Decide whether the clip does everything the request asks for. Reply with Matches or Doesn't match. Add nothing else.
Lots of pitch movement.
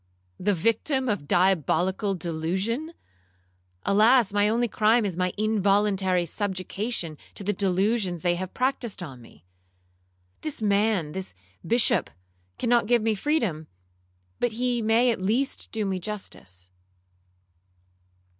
Doesn't match